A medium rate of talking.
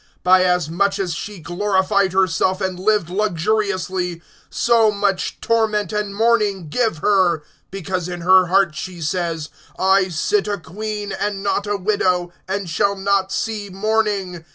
Yes: average, 150 wpm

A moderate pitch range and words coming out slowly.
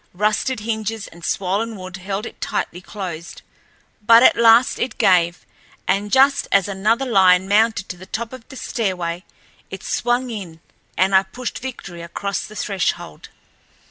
No: average, 3.6 semitones; average, 155 wpm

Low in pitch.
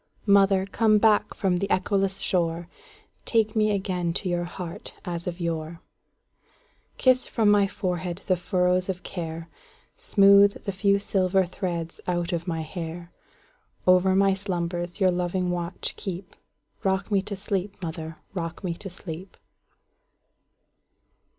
No: medium, 185 Hz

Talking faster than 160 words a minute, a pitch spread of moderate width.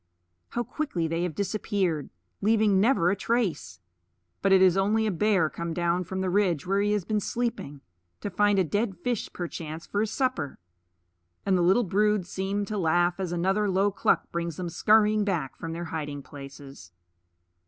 Yes: average, 180 wpm; average, 3.6 semitones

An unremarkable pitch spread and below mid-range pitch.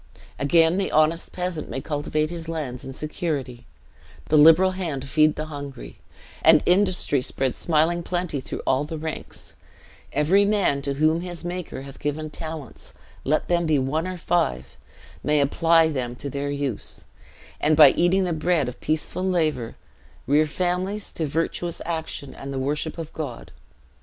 No: average, 3.4 semitones; medium, 155 Hz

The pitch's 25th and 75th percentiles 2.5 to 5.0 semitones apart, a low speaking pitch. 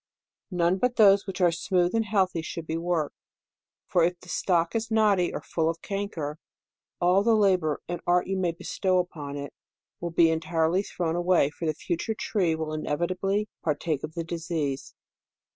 No: average, 2.9 semitones; medium, 175 Hz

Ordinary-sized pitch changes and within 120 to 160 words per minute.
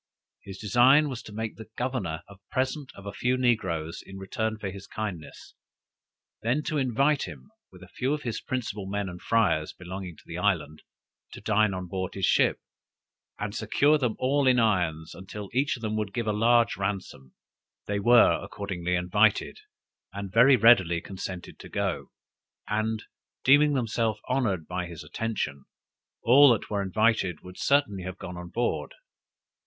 No: average, 4.7 semitones; average, 170 wpm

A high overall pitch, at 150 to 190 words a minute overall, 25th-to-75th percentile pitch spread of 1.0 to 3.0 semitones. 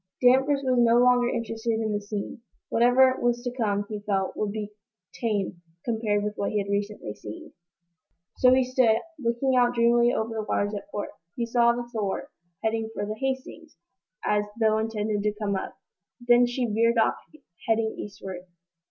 Yes: high, 225 Hz; average, 175 wpm; average, 2.7 semitones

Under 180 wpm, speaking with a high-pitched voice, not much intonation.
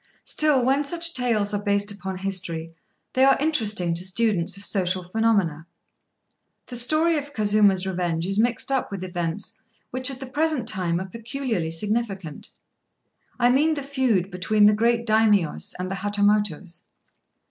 No: average, 155 wpm; high, 210 Hz; average, 5.2 semitones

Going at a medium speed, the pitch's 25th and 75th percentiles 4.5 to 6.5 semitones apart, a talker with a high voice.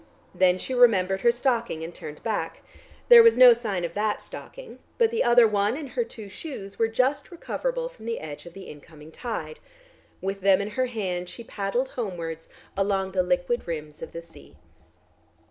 Yes: average, 185 wpm; wide, 5.4 semitones; high, 205 Hz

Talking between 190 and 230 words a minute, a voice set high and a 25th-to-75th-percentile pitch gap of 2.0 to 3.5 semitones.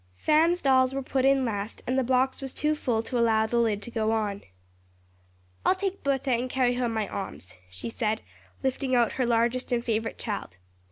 Yes: fast, 205 wpm; high, 245 Hz; average, 3.1 semitones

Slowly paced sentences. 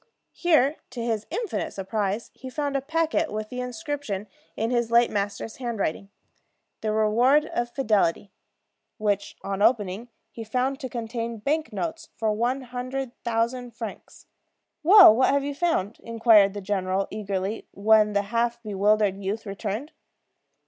No: average, 145 wpm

